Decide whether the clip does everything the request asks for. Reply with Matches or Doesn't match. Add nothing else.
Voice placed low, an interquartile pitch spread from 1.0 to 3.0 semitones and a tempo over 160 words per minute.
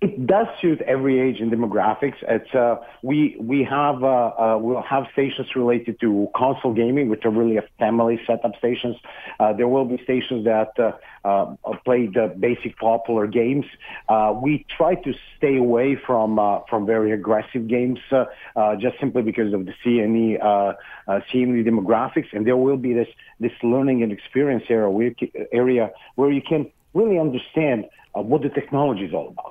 Matches